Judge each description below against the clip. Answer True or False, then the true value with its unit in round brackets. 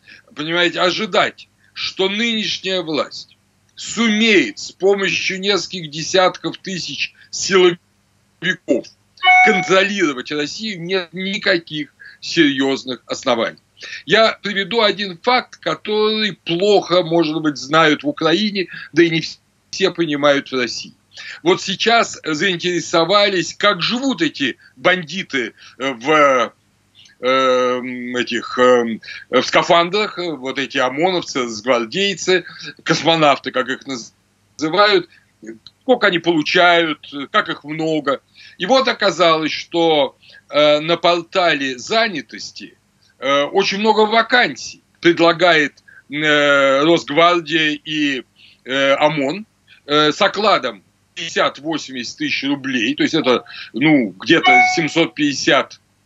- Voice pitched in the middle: True (170 Hz)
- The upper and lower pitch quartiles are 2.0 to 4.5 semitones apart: False (5.6 semitones)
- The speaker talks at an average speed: False (90 wpm)